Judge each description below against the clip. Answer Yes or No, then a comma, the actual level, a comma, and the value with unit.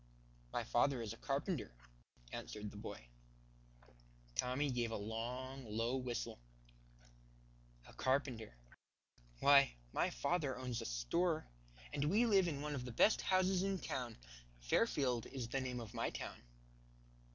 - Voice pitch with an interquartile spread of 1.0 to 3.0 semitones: No, average, 4.1 semitones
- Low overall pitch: Yes, low, 125 Hz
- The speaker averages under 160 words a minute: Yes, average, 140 wpm